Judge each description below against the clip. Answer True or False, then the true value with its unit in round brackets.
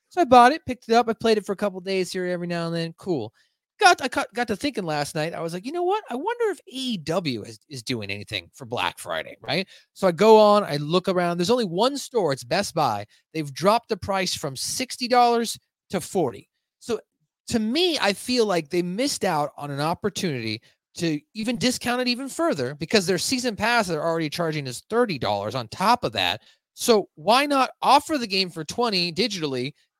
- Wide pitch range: True (7.1 semitones)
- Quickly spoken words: True (220 wpm)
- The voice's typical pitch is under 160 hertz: False (200 Hz)